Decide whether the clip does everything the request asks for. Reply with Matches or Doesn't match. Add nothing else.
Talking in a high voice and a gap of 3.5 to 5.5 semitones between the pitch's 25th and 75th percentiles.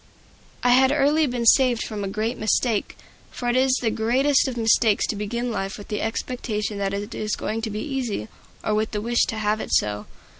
Doesn't match